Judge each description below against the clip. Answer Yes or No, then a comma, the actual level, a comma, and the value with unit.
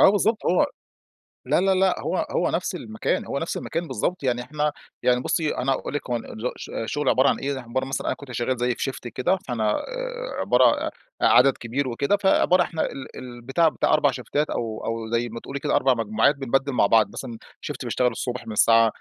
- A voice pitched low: Yes, low, 130 Hz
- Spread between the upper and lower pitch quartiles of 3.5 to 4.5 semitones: Yes, average, 4.1 semitones